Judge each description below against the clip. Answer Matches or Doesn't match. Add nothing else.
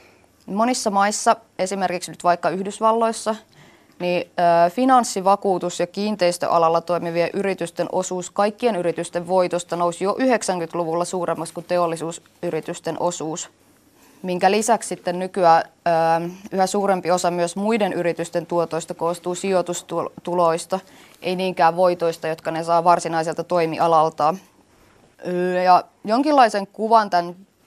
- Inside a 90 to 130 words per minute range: Matches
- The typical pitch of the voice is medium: Matches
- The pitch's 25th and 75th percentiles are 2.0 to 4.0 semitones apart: Matches